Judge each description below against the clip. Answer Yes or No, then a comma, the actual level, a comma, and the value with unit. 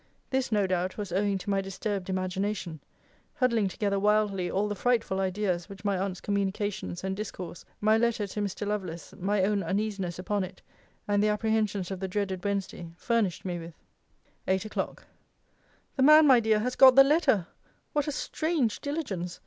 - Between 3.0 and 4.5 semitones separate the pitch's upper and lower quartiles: No, narrow, 2.4 semitones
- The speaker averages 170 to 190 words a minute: Yes, average, 175 wpm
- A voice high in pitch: Yes, high, 200 Hz